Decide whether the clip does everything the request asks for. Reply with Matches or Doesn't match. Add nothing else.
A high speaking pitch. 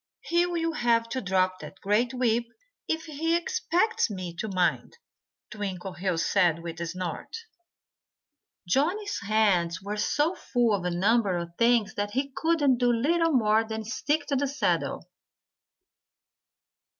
Matches